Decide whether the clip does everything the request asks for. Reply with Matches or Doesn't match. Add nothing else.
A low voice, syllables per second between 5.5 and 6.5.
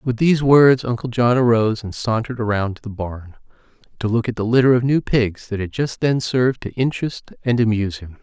Matches